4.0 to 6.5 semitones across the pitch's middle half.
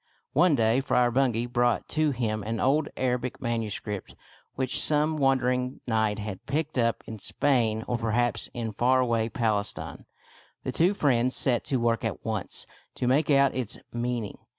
No: average, 2.9 semitones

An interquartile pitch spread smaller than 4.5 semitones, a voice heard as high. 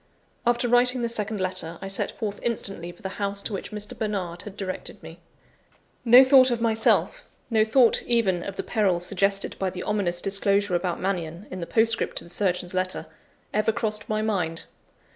Yes: average, 3.3 semitones; high, 200 Hz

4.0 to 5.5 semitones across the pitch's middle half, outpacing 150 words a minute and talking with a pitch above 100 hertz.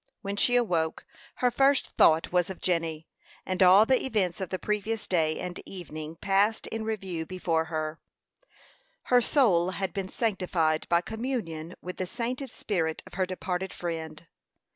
Yes: average, 4.7 semitones; average, 160 wpm; medium, 185 Hz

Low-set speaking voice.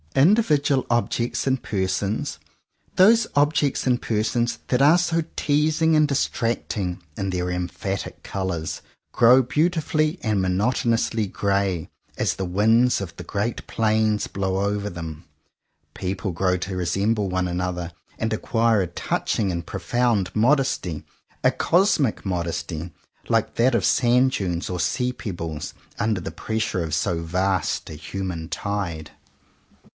Yes: low, 105 Hz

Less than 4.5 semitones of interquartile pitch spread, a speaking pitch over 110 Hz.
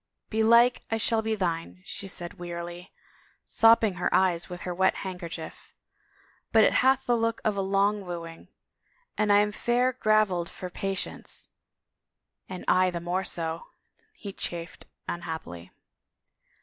Yes: average, 3.9 semitones; high, 190 Hz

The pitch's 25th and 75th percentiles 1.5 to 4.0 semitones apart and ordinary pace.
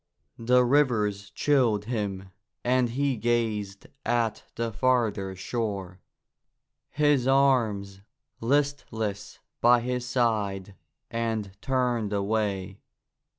No: average, 3.7 semitones; slow, 90 wpm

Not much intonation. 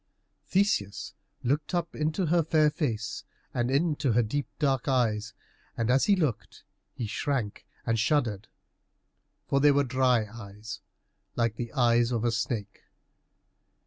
No: average, 4.6 semitones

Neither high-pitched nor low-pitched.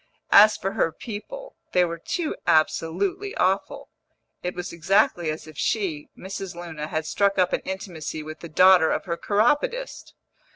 Yes: medium, 180 Hz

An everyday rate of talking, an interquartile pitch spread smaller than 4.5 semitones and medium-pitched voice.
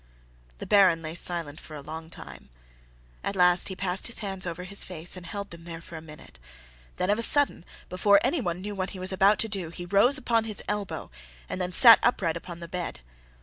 No: fast, 220 wpm; average, 3.2 semitones; medium, 180 Hz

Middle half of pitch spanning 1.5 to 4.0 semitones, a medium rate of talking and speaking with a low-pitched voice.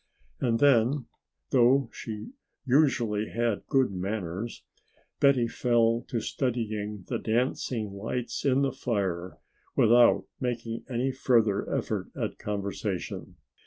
No: average, 3.2 semitones; slow, 110 wpm; low, 115 Hz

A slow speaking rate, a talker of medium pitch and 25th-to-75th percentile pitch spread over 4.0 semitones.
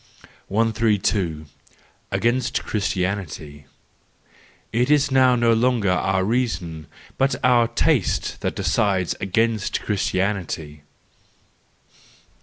No: slow, 80 wpm; low, 105 Hz; average, 4.4 semitones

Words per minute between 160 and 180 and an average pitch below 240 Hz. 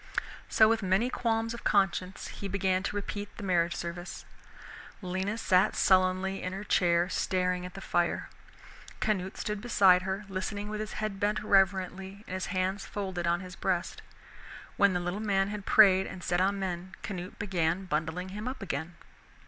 Yes: average, 170 wpm; high, 190 Hz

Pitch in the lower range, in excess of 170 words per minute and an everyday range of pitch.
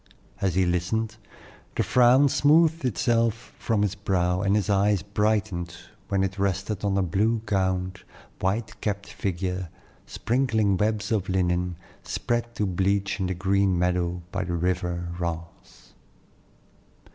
No: low, 100 Hz; slow, 135 wpm; average, 3.1 semitones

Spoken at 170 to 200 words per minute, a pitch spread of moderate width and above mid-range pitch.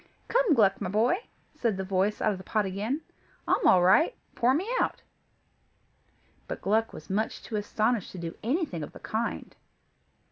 Yes: average, 175 wpm; average, 4.4 semitones; high, 215 Hz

